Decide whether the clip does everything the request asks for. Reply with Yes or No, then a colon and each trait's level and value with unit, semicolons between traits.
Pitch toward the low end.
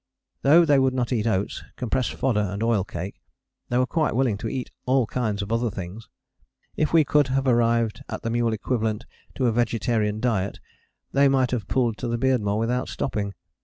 Yes: low, 120 Hz